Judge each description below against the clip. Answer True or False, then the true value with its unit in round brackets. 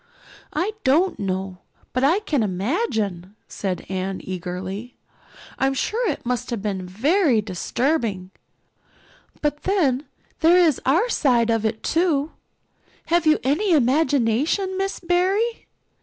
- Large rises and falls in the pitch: True (8.8 semitones)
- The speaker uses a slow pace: True (125 wpm)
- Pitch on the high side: True (265 Hz)